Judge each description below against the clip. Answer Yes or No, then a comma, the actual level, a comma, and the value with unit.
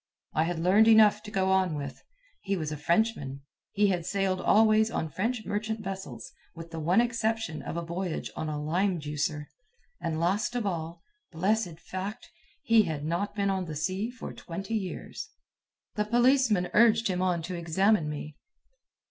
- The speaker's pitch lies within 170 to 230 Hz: Yes, high, 190 Hz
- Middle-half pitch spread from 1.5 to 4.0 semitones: No, average, 4.7 semitones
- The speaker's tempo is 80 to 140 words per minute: No, average, 175 wpm